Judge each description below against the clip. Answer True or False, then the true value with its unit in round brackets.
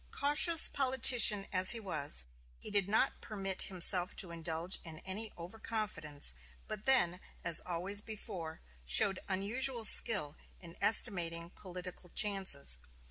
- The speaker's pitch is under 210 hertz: True (190 Hz)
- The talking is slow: True (130 wpm)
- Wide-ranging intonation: False (4.3 semitones)